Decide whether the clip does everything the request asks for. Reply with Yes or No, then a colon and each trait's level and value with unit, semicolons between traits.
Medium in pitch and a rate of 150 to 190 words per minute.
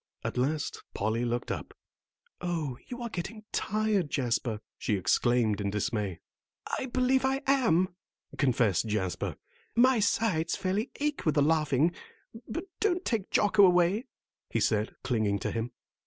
No: medium, 160 Hz; average, 140 wpm